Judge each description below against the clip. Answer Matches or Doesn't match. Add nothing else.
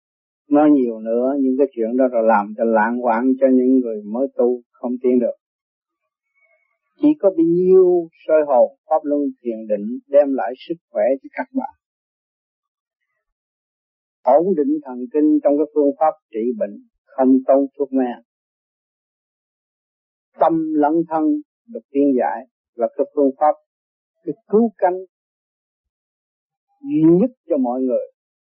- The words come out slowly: Matches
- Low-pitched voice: Doesn't match